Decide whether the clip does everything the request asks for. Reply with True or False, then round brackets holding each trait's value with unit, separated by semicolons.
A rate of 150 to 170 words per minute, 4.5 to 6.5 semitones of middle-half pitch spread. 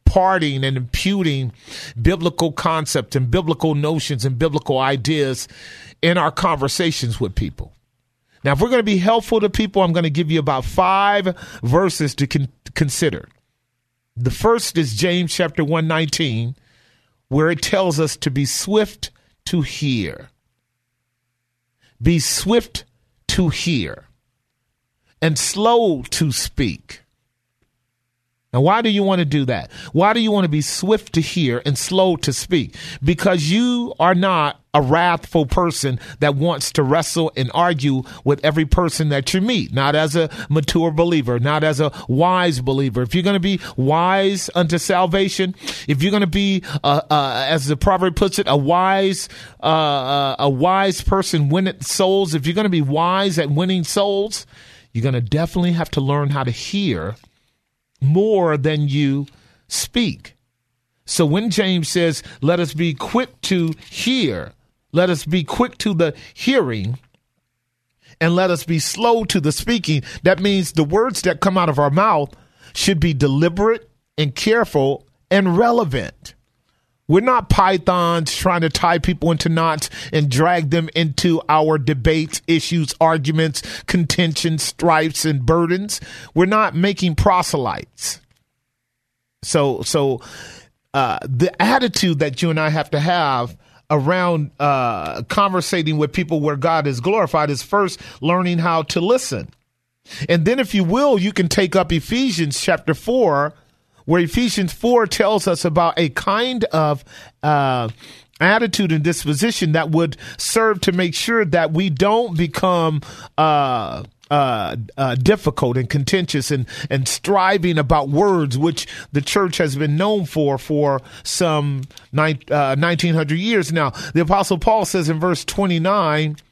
True (155 wpm; 4.9 semitones)